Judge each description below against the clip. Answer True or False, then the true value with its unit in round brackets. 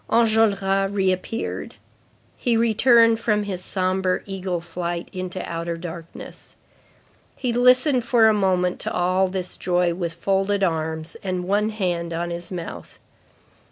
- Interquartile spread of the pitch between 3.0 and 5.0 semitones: True (3.3 semitones)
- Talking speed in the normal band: False (130 wpm)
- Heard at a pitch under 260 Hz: True (185 Hz)